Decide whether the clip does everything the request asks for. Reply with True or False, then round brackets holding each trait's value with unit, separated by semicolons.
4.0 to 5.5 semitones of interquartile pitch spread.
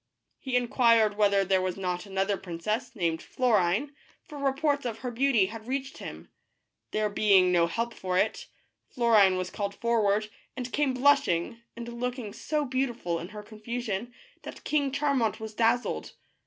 True (4.3 semitones)